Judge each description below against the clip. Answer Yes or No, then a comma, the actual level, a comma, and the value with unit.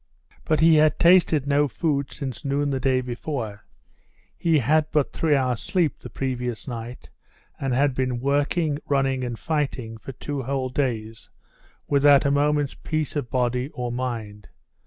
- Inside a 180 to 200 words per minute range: No, average, 155 wpm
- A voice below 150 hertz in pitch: Yes, low, 135 Hz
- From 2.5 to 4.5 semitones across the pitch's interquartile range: Yes, average, 2.8 semitones